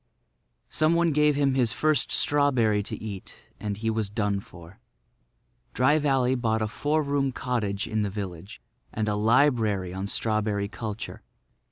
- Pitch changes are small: No, average, 5.0 semitones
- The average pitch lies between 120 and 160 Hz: No, low, 110 Hz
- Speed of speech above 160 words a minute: No, average, 155 wpm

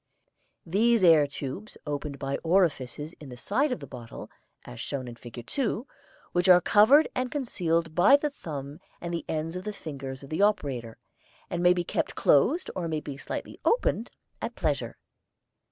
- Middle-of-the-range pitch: Yes, medium, 165 Hz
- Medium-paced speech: Yes, average, 175 wpm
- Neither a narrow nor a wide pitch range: No, wide, 6.7 semitones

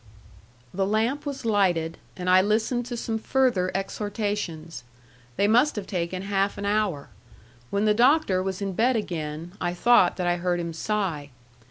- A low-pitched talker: No, high, 195 Hz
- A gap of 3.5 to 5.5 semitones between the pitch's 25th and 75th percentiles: Yes, average, 3.8 semitones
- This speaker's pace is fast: No, average, 165 wpm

